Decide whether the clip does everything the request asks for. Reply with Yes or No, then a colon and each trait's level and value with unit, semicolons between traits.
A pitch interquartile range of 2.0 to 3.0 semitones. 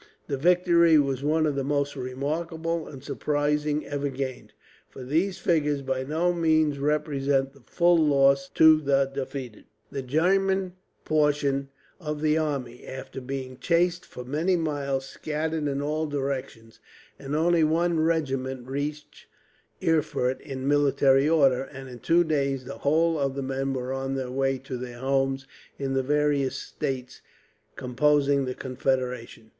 Yes: average, 2.7 semitones